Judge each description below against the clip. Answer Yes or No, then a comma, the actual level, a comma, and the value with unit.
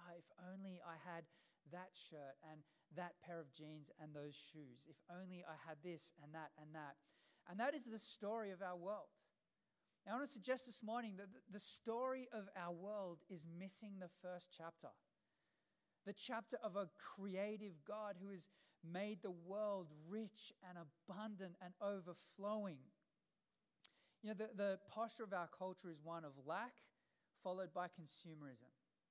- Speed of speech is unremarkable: Yes, average, 165 wpm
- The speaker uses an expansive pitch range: No, average, 3.8 semitones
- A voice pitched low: No, medium, 185 Hz